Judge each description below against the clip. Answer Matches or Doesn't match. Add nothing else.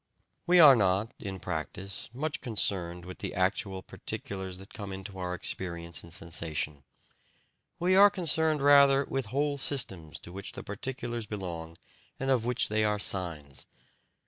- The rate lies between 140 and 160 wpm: Matches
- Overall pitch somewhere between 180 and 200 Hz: Doesn't match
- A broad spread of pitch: Matches